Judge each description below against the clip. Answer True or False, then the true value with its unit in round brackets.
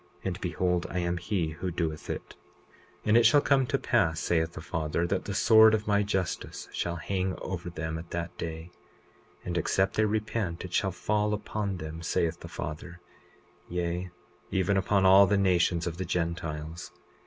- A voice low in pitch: True (90 Hz)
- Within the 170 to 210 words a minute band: True (180 wpm)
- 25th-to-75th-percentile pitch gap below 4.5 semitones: True (2.9 semitones)